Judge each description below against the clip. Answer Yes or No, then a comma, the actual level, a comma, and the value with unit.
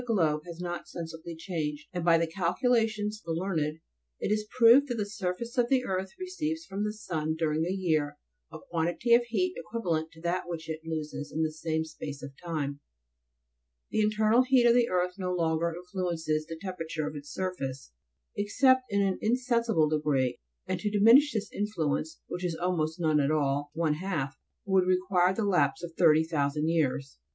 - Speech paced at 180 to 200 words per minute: Yes, average, 185 wpm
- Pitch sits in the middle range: Yes, medium, 175 Hz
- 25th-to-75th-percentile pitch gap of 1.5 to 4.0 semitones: No, average, 5.0 semitones